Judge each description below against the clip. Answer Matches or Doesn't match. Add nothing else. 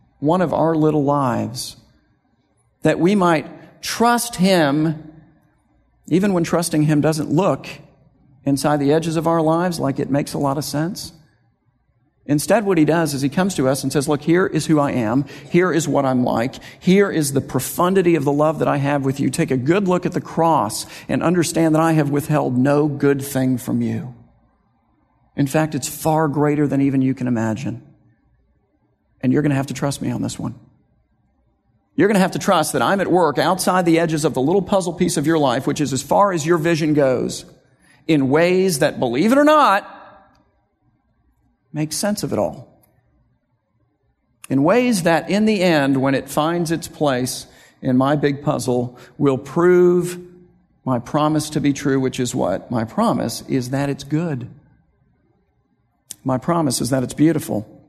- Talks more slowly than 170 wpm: Doesn't match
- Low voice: Doesn't match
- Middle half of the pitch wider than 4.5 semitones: Doesn't match